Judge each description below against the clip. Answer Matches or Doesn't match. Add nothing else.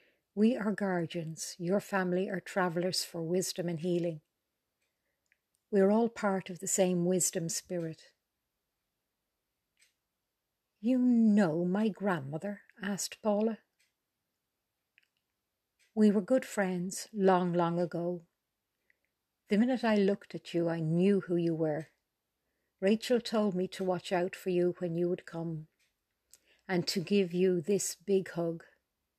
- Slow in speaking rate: Matches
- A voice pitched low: Doesn't match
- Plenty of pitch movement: Doesn't match